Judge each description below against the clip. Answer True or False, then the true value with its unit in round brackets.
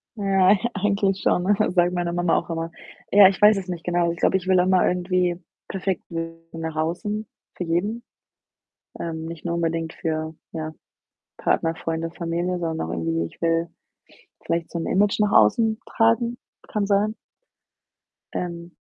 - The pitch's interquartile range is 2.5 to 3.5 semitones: True (2.8 semitones)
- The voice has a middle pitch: True (175 Hz)